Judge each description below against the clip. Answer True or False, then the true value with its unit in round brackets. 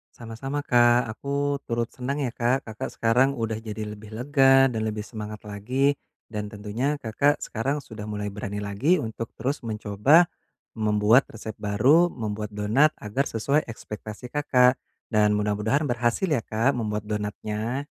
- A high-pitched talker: False (115 Hz)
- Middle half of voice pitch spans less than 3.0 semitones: False (4.2 semitones)